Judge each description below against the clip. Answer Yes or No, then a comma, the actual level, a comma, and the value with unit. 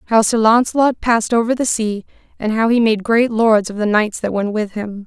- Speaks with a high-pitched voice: Yes, high, 220 Hz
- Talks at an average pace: No, fast, 235 wpm